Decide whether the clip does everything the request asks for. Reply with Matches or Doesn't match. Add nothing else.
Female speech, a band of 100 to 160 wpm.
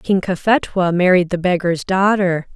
Matches